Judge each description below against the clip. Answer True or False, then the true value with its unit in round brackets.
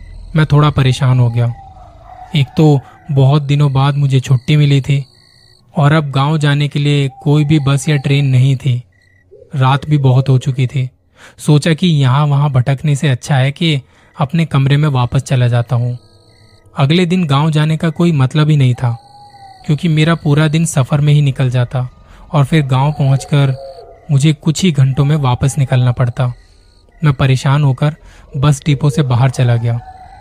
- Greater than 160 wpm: True (175 wpm)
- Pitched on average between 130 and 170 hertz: True (140 Hz)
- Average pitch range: True (3.0 semitones)